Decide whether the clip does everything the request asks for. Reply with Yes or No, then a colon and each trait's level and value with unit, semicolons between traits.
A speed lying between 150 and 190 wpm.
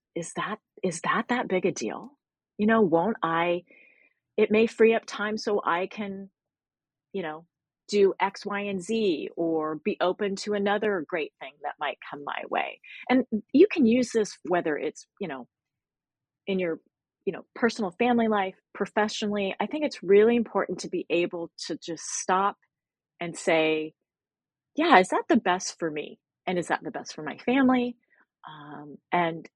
Yes: average, 175 wpm